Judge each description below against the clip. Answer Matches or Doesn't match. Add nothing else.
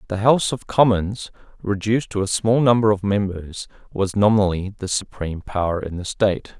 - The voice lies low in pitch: Matches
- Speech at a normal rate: Matches